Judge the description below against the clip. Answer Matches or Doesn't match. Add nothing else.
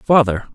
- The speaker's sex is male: Matches